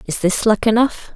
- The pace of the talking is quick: Yes, fast, 210 wpm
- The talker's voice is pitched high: Yes, high, 215 Hz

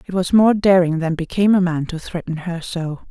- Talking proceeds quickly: Yes, fast, 230 wpm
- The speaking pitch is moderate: Yes, medium, 175 Hz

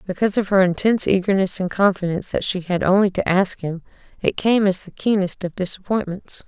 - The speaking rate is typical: Yes, average, 195 wpm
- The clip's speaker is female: Yes, female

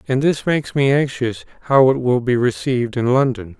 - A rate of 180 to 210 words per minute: Yes, average, 200 wpm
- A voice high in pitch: No, low, 130 Hz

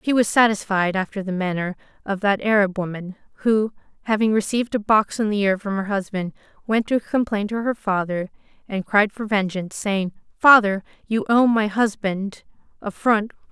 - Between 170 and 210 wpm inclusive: Yes, average, 180 wpm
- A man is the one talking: No, female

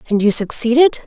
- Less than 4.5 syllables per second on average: No, 5.8 syllables/s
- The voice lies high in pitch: Yes, high, 240 Hz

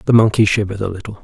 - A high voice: No, low, 105 Hz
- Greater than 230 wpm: Yes, fast, 245 wpm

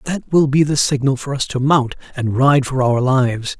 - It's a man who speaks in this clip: Yes, male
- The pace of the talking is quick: Yes, fast, 235 wpm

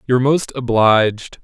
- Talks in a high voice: No, low, 120 Hz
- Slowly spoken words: Yes, slow, 125 wpm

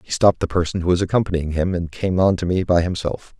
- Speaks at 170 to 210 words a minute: No, fast, 265 wpm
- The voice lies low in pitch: Yes, very low, 90 Hz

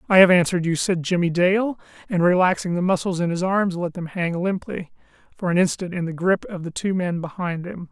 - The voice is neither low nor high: Yes, medium, 180 Hz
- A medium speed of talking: No, fast, 220 wpm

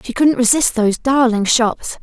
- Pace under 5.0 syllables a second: Yes, 4.8 syllables/s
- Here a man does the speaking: No, female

